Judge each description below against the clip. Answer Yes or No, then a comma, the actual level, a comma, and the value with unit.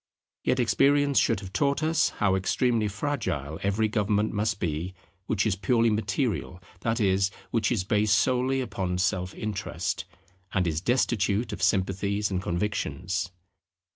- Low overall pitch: Yes, low, 105 Hz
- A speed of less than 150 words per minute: Yes, average, 140 wpm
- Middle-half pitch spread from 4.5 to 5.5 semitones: No, average, 3.6 semitones